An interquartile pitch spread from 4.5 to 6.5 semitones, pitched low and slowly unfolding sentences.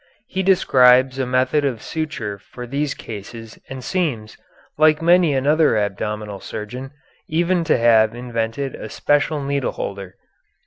Yes: average, 5.2 semitones; low, 130 Hz; slow, 130 wpm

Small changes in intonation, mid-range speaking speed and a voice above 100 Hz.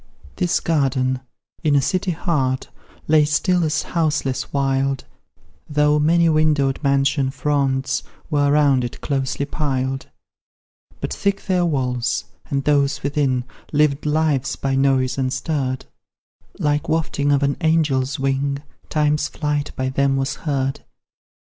No: narrow, 2.1 semitones; slow, 125 wpm; medium, 140 Hz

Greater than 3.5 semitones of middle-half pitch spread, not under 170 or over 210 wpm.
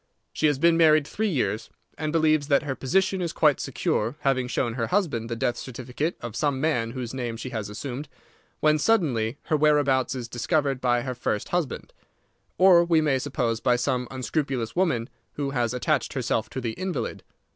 Yes: average, 4.3 semitones; average, 185 wpm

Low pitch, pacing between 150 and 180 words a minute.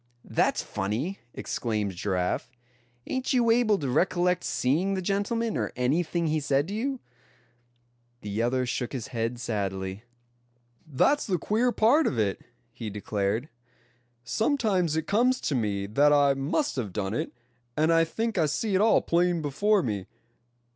No: medium, 150 Hz; average, 155 wpm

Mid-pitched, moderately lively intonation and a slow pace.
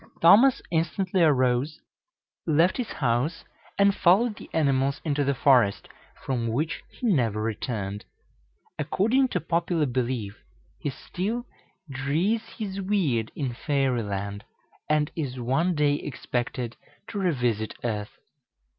No: medium, 145 Hz; wide, 6.5 semitones; slow, 120 wpm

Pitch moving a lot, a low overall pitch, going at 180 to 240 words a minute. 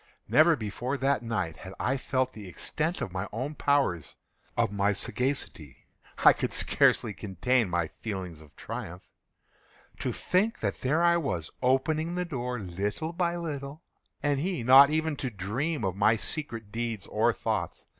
No: wide, 7.1 semitones; low, 125 Hz; average, 155 wpm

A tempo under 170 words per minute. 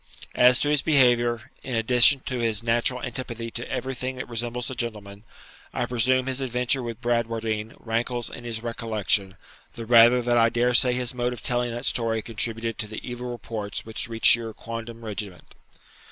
No: average, 175 wpm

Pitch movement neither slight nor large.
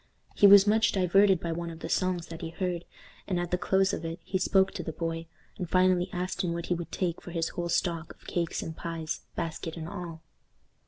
No: narrow, 2.0 semitones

